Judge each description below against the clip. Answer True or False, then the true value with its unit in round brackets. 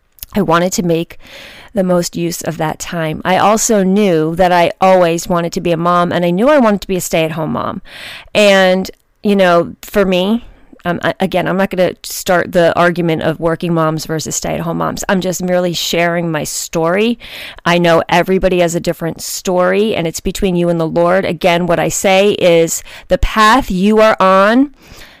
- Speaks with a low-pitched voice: False (180 Hz)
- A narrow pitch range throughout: True (2.3 semitones)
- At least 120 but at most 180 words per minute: False (195 wpm)